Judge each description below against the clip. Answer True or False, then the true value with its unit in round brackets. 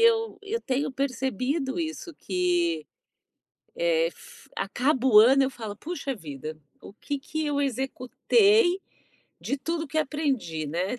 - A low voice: False (270 Hz)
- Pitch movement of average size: False (6.9 semitones)